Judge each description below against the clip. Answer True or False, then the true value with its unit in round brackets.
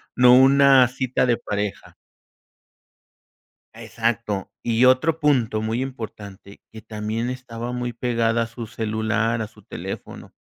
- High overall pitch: False (115 Hz)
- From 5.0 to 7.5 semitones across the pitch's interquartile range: False (2.4 semitones)